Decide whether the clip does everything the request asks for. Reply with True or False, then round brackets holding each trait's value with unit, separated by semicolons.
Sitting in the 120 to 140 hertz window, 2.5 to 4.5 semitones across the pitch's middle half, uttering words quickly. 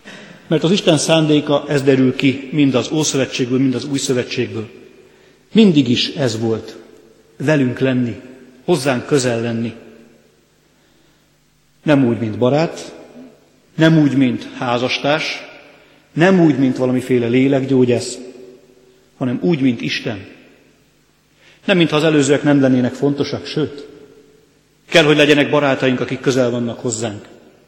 False (135 Hz; 2.8 semitones; 120 wpm)